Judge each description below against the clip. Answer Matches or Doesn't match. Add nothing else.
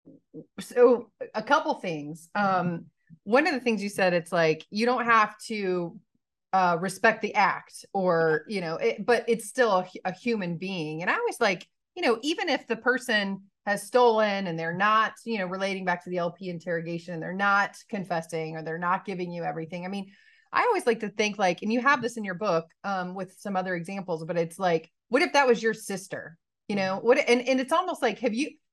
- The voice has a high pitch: Matches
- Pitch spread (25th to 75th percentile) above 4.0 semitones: Matches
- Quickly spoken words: Matches